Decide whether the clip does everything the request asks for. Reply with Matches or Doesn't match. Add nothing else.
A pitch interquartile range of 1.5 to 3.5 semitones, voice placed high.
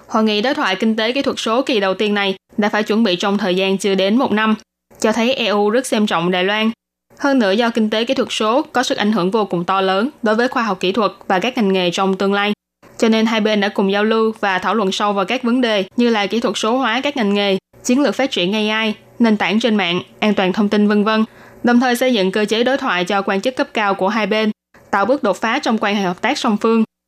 Matches